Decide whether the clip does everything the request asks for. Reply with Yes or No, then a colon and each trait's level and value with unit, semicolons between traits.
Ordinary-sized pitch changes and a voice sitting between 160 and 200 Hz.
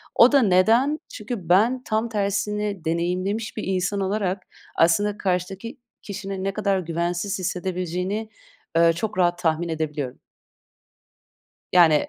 Yes: average, 3.2 semitones; high, 190 Hz